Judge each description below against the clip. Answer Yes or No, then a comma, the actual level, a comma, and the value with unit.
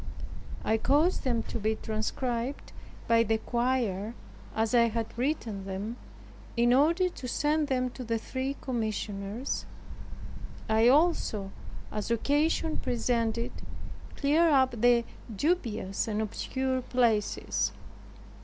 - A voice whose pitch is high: Yes, high, 235 Hz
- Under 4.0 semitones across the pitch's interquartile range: Yes, average, 3.3 semitones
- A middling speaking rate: No, slow, 115 wpm